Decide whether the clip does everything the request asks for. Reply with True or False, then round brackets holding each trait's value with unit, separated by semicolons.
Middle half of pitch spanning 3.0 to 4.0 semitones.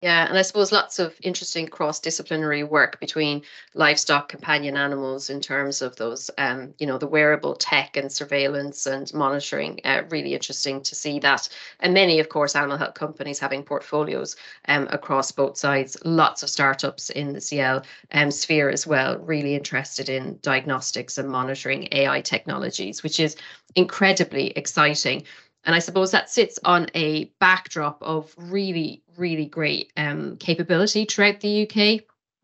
True (3.3 semitones)